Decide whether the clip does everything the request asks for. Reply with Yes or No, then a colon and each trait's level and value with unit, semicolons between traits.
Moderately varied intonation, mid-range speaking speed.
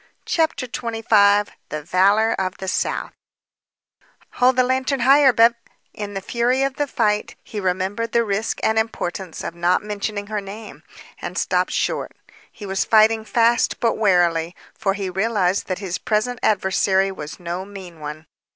Yes: average, 3.4 semitones; average, 160 wpm